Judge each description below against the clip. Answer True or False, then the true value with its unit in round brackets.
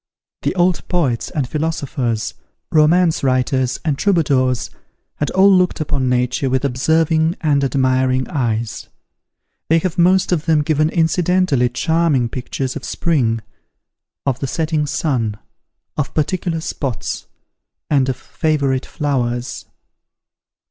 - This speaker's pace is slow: True (120 wpm)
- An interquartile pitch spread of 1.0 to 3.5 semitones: False (4.1 semitones)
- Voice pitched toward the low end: False (145 Hz)